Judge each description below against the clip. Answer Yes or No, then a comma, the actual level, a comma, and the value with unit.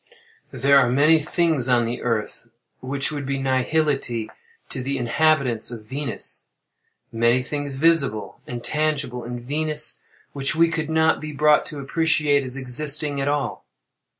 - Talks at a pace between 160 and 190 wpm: No, average, 145 wpm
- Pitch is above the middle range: No, medium, 140 Hz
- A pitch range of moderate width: Yes, average, 3.4 semitones